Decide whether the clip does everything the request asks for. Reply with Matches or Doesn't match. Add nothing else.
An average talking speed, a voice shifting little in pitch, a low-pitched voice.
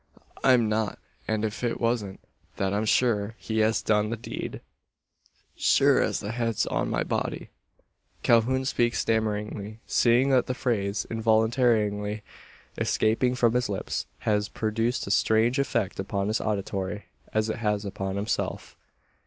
Matches